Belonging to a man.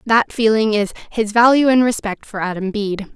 No: female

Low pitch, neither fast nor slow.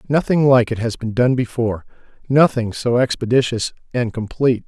Yes: low, 120 Hz; average, 155 wpm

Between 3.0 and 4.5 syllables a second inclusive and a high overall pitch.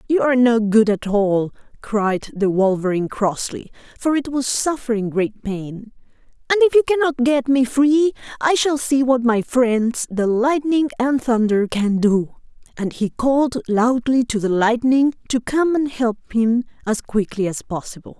Yes: 4.4 syllables/s; high, 240 Hz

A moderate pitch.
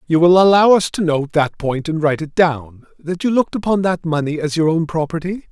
Yes: medium, 165 Hz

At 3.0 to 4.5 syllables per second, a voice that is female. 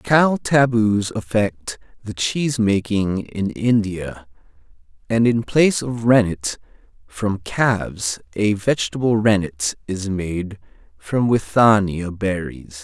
No: 3.6 syllables/s; male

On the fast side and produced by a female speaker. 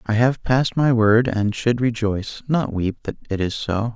No: fast, 210 wpm; male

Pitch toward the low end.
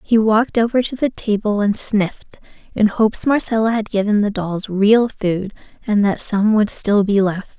No: high, 210 Hz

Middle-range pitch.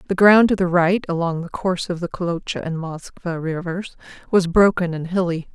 Yes: medium, 175 Hz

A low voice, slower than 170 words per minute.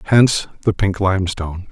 Yes: very low, 95 Hz; average, 140 wpm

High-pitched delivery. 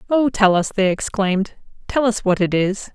Yes: high, 205 Hz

